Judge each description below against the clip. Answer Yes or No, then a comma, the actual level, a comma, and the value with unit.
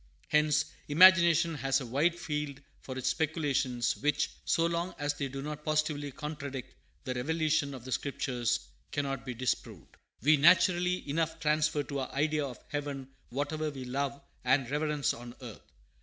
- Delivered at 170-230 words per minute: No, average, 155 wpm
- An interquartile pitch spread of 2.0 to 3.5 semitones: Yes, narrow, 2.6 semitones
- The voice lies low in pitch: No, medium, 145 Hz